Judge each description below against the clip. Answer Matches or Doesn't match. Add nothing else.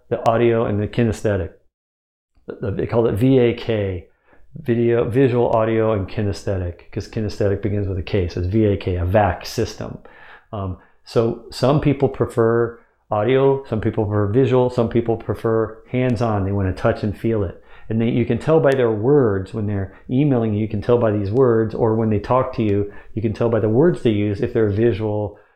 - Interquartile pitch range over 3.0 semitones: Doesn't match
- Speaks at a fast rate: Doesn't match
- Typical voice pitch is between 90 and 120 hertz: Matches